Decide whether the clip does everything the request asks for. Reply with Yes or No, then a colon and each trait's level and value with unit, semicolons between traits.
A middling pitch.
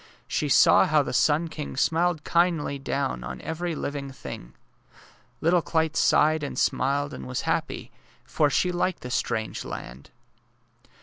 Yes: medium, 150 Hz